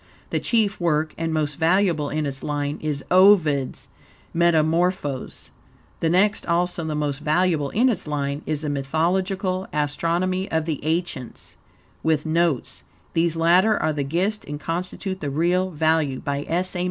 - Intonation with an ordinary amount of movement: Yes, average, 3.5 semitones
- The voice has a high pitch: No, medium, 160 Hz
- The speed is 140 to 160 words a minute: Yes, average, 155 wpm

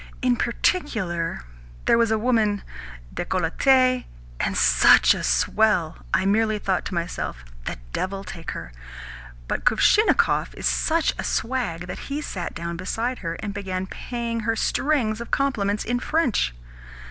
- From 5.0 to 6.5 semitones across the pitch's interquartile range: Yes, wide, 5.5 semitones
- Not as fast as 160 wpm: Yes, average, 145 wpm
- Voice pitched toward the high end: Yes, high, 215 Hz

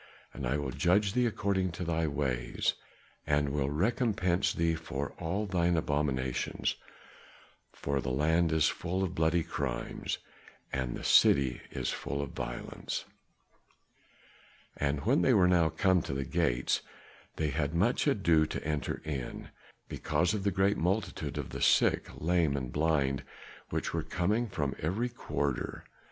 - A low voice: Yes, very low, 80 Hz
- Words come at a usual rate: Yes, average, 150 wpm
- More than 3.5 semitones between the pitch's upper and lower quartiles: Yes, average, 4.6 semitones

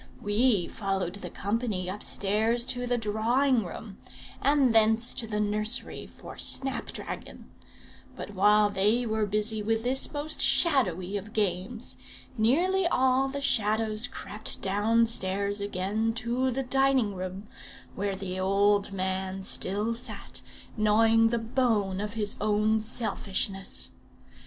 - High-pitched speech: Yes, high, 215 Hz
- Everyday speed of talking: No, slow, 130 wpm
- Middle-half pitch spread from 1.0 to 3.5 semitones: Yes, average, 3.0 semitones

